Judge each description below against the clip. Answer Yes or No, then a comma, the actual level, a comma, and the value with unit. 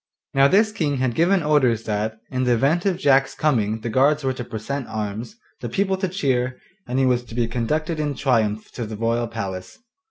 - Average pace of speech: No, fast, 210 wpm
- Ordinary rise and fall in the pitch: Yes, average, 4.8 semitones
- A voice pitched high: No, low, 130 Hz